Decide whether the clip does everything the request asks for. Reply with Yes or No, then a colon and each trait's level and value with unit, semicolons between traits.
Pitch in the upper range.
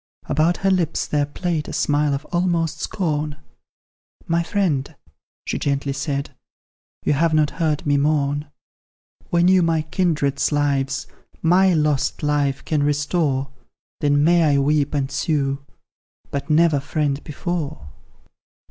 No: medium, 150 Hz